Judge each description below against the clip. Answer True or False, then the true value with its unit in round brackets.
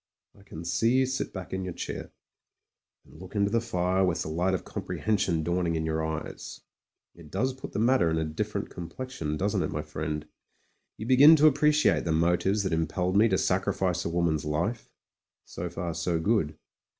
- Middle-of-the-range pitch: False (90 Hz)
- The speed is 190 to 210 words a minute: True (200 wpm)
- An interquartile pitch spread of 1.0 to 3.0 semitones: False (4.7 semitones)